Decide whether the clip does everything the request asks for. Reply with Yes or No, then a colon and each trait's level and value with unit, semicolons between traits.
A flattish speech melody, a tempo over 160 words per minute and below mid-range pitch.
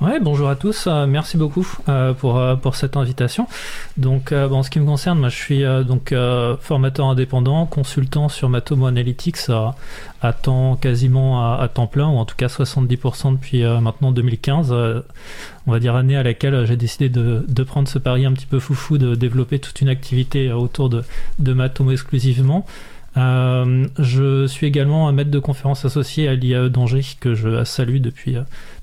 Yes: narrow, 2.1 semitones; average, 200 wpm; low, 130 Hz